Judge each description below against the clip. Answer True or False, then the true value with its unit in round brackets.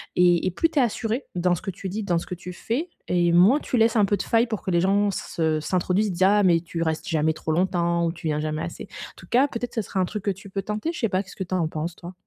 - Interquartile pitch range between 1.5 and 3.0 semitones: False (3.7 semitones)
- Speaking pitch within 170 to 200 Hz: True (185 Hz)